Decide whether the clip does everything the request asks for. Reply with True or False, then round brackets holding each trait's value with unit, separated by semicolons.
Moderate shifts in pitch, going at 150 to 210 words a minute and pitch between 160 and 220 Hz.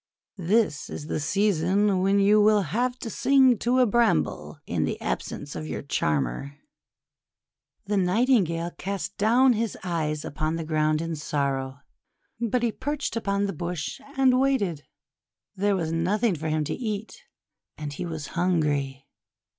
False (6.2 semitones; 155 wpm; 185 Hz)